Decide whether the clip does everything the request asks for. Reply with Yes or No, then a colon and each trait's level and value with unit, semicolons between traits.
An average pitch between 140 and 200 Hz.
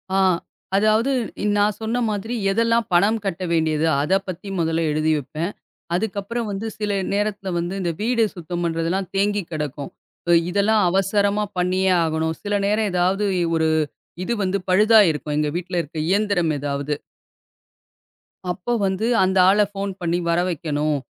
Yes: high, 190 Hz